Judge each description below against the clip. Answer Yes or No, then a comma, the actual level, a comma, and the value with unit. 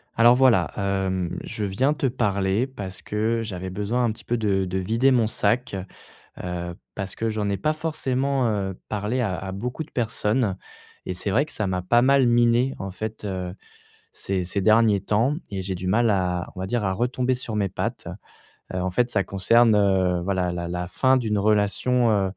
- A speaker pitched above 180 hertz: No, low, 105 Hz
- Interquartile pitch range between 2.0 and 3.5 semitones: No, average, 4.0 semitones